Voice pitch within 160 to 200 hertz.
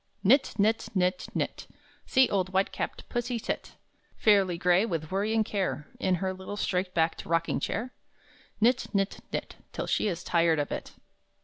Yes: high, 190 Hz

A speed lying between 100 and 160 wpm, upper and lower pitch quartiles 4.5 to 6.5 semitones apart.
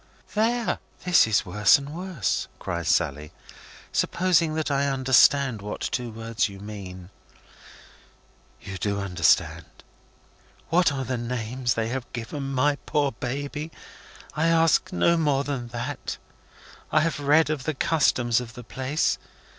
Yes: average, 140 wpm; average, 5.2 semitones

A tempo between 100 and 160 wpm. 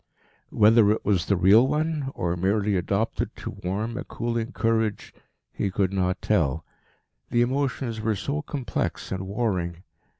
Yes: average, 145 wpm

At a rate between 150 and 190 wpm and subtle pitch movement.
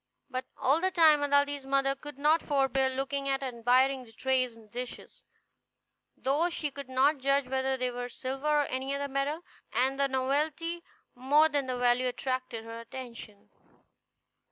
Yes: average, 165 wpm; narrow, 2.0 semitones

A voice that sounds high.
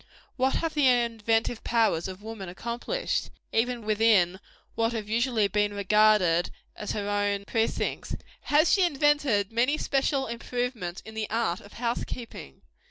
Yes: high, 225 Hz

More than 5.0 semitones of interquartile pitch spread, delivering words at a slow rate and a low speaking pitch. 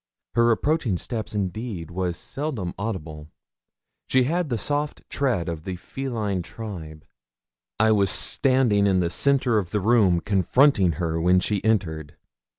No: wide, 5.6 semitones; average, 145 wpm; low, 100 Hz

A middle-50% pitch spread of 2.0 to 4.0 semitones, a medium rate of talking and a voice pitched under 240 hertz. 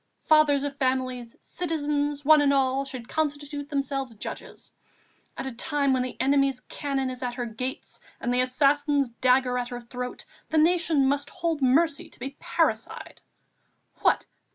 No: narrow, 2.4 semitones; average, 155 wpm; very high, 275 Hz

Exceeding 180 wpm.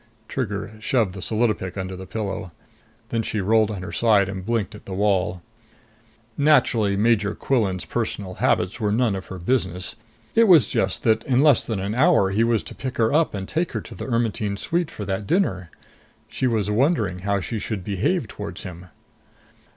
Yes: average, 190 wpm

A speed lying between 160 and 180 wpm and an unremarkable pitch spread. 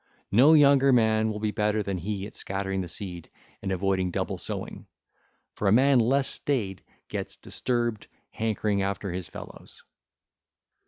No: average, 150 wpm; average, 3.6 semitones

